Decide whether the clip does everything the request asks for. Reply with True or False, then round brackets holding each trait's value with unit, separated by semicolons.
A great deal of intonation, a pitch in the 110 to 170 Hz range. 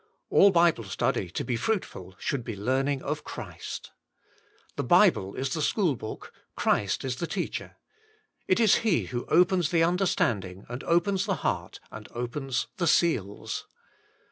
True (7.1 semitones; 140 Hz)